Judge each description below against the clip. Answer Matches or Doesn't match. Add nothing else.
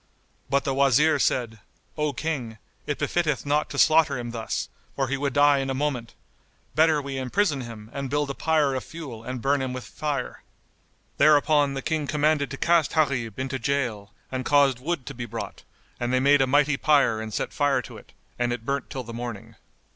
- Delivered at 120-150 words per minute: Doesn't match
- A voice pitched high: Doesn't match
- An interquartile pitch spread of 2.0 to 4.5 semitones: Matches